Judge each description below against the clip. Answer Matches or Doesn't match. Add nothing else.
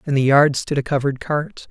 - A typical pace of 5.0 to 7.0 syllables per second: Matches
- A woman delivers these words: Doesn't match